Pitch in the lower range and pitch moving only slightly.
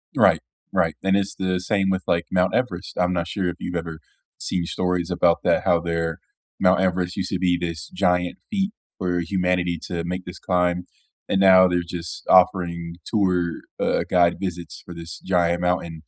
Yes: very low, 90 Hz; narrow, 1.3 semitones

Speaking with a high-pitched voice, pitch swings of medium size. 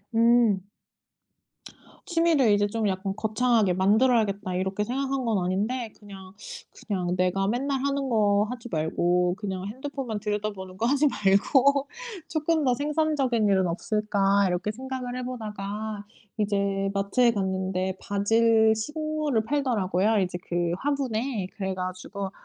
Yes: high, 215 Hz; average, 4.5 semitones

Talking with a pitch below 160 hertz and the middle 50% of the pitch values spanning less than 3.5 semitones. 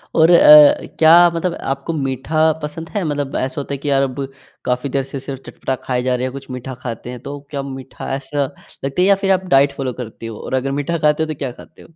Yes: medium, 140 Hz; narrow, 2.5 semitones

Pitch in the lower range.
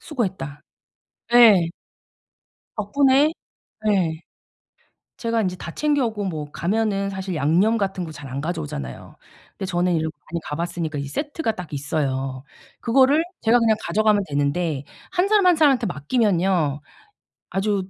No: high, 190 Hz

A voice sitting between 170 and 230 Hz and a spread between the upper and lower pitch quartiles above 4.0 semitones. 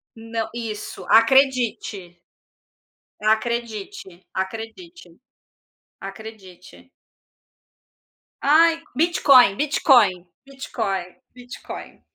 Yes: high, 225 Hz; wide, 5.4 semitones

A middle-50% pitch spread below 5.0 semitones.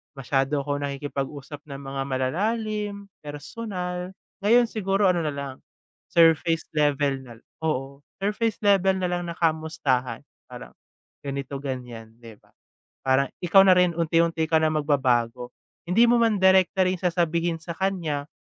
No: average, 5.3 semitones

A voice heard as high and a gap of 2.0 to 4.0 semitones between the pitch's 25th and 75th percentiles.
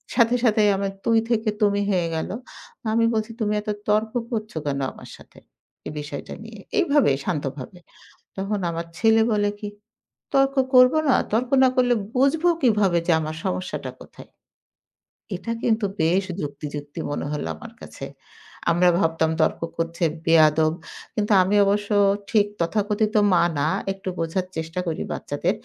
No: high, 200 Hz; average, 5.1 semitones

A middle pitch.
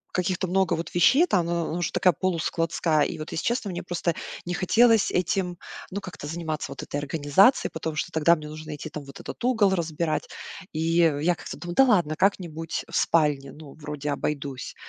Yes: medium, 165 Hz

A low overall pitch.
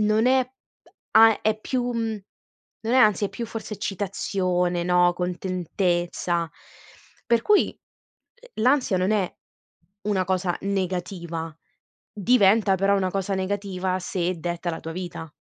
No: high, 190 Hz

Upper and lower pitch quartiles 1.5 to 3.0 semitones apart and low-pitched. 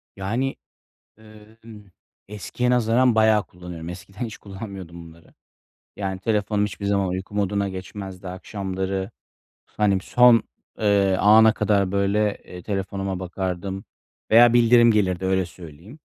Yes: narrow, 2.5 semitones; low, 100 Hz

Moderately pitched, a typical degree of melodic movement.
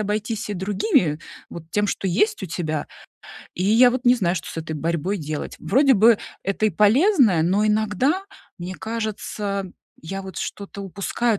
No: high, 205 Hz; average, 3.7 semitones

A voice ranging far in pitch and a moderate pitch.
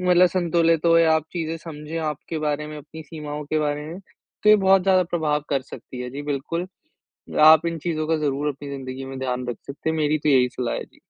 No: narrow, 2.6 semitones; medium, 150 Hz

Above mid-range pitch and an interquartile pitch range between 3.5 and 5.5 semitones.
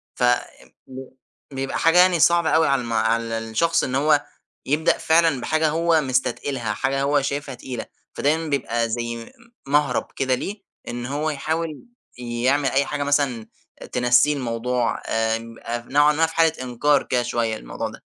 No: low, 135 Hz; average, 4.0 semitones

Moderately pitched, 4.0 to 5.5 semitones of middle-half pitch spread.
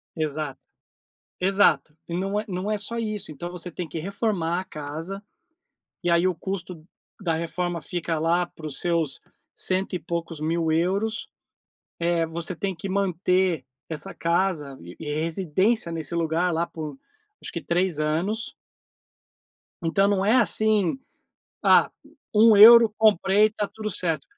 No: medium, 175 Hz; average, 3.4 semitones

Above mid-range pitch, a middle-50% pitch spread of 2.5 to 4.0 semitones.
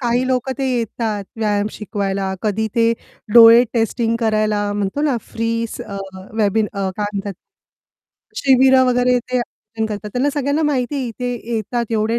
Yes: high, 230 Hz; average, 3.0 semitones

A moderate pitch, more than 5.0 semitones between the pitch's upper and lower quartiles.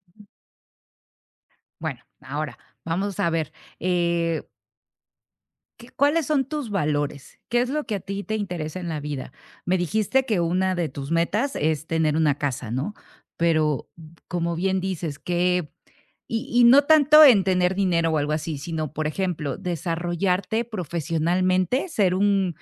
No: medium, 175 Hz; average, 4.2 semitones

